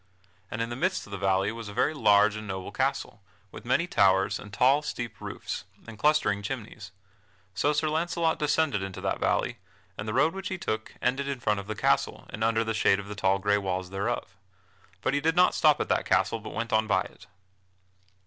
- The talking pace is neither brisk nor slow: No, fast, 215 wpm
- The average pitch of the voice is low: Yes, low, 110 Hz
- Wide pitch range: Yes, wide, 6.1 semitones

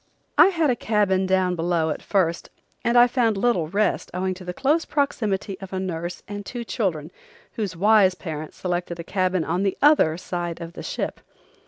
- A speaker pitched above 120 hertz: Yes, high, 190 Hz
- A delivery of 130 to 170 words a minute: No, average, 190 wpm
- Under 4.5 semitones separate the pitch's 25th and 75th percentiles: Yes, average, 3.8 semitones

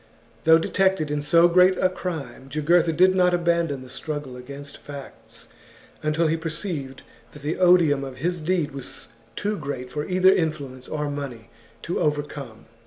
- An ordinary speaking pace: Yes, average, 160 wpm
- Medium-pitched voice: Yes, medium, 155 Hz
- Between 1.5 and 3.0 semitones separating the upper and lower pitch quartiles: No, average, 3.7 semitones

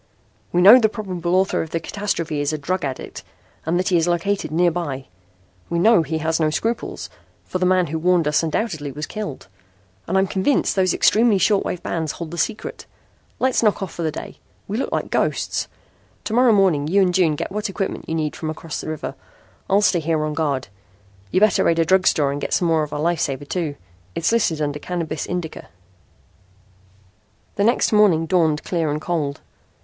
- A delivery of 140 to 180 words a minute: No, fast, 205 wpm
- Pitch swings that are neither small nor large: Yes, average, 3.7 semitones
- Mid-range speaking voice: Yes, medium, 170 Hz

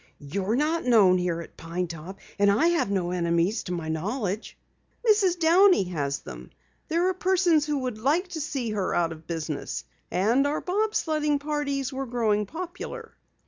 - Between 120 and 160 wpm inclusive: No, average, 175 wpm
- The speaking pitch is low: No, high, 240 Hz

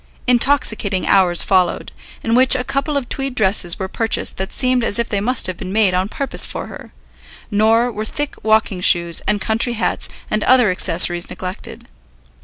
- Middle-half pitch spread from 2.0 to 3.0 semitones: No, average, 4.7 semitones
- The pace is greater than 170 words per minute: Yes, average, 180 wpm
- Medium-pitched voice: No, high, 215 Hz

